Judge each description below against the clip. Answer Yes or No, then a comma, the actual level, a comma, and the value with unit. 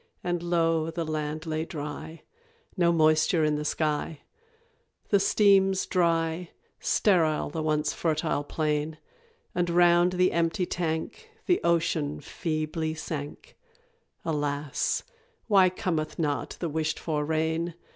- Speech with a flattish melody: Yes, narrow, 2.1 semitones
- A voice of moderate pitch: Yes, medium, 160 Hz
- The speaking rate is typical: No, slow, 120 wpm